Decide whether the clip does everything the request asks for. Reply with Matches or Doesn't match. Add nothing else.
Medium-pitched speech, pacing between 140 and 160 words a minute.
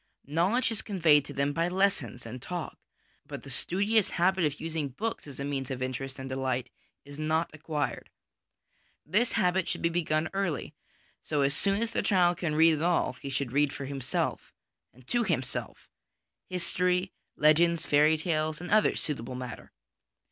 Doesn't match